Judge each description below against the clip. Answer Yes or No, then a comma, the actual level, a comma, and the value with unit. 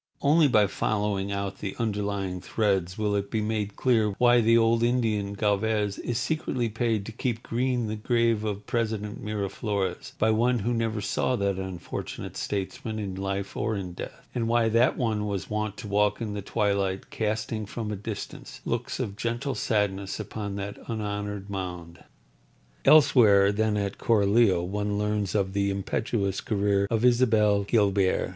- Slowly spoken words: No, average, 165 wpm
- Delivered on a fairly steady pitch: Yes, narrow, 2.3 semitones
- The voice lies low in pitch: Yes, low, 105 Hz